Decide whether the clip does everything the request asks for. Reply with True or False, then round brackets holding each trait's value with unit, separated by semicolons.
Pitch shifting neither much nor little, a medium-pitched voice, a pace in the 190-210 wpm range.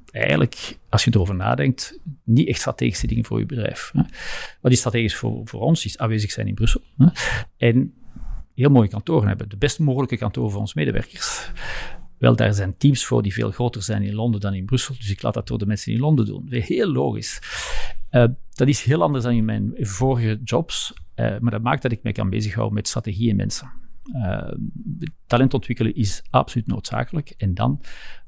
False (3.3 semitones; 115 Hz; 195 wpm)